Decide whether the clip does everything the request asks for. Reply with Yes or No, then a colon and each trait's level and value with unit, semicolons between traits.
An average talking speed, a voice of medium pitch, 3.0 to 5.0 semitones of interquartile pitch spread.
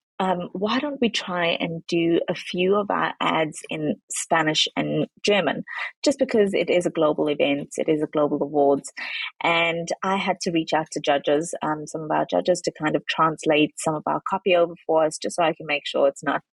No: fast, 220 wpm; medium, 165 Hz; average, 3.3 semitones